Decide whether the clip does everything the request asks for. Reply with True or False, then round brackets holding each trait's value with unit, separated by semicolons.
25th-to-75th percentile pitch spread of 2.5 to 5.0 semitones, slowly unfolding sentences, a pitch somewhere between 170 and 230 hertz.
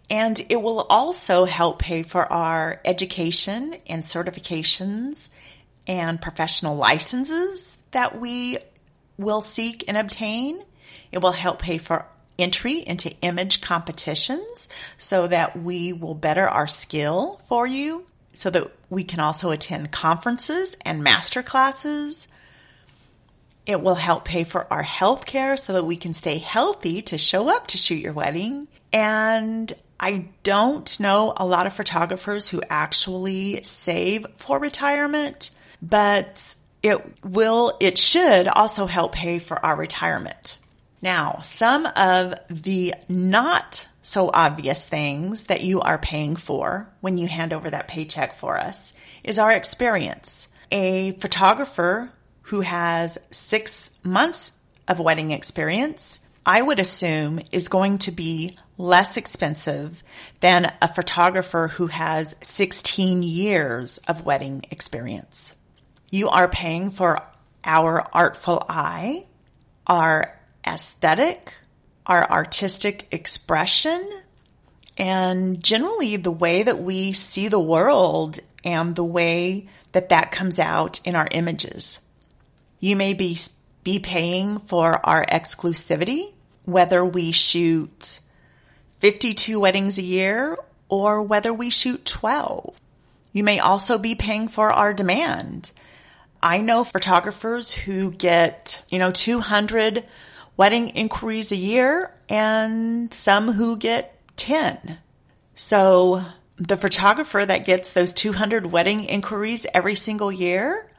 True (4.2 semitones; 125 wpm; 185 Hz)